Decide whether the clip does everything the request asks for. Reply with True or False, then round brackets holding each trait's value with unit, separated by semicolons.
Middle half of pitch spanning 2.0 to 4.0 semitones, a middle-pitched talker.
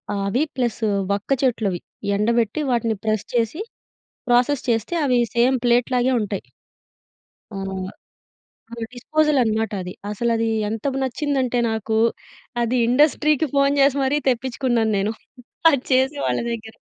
False (3.2 semitones; 240 Hz)